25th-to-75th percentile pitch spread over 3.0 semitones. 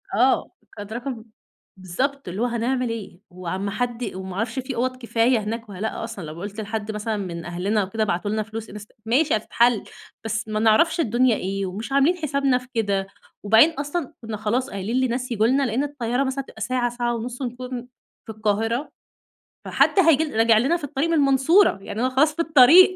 Yes: average, 3.9 semitones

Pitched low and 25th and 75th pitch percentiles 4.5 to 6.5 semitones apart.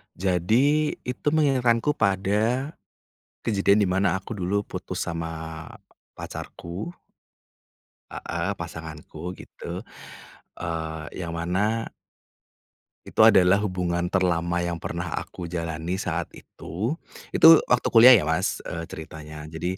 Yes: very low, 90 Hz; average, 4.8 semitones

